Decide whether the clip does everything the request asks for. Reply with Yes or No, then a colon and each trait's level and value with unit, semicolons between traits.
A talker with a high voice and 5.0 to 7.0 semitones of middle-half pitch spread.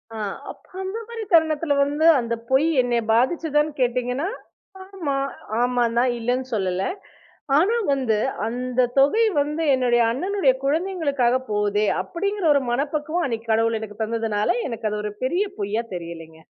Yes: very high, 255 Hz; average, 5.3 semitones